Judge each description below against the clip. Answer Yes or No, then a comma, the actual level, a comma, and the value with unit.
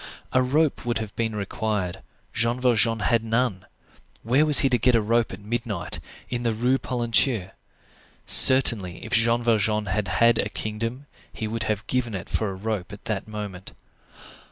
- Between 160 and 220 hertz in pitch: No, low, 115 Hz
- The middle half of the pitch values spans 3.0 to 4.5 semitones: No, narrow, 2.4 semitones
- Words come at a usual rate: Yes, average, 175 wpm